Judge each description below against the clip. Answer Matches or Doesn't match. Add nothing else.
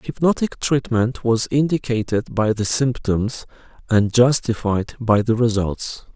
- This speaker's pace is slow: Matches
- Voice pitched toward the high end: Doesn't match